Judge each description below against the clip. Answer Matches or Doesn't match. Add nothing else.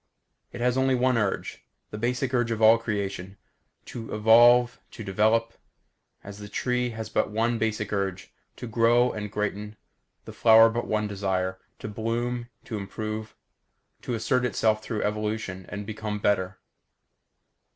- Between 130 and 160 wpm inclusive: Matches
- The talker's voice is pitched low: Matches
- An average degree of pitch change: Doesn't match